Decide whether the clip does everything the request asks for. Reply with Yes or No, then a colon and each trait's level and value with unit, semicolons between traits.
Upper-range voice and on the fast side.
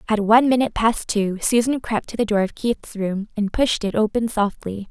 Yes: high, 215 Hz; fast, 220 wpm